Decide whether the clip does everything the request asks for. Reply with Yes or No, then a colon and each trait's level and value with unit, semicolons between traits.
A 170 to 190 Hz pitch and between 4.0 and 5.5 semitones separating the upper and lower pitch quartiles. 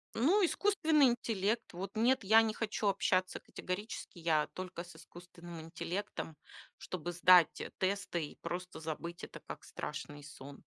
Yes: medium, 185 Hz; average, 4.4 semitones